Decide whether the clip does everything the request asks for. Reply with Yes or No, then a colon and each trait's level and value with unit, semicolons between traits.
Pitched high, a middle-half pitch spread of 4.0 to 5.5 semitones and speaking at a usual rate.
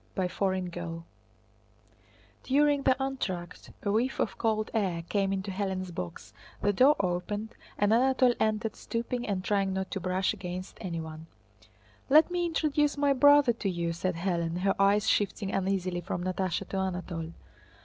Yes: high, 195 Hz; average, 4.4 semitones; average, 150 wpm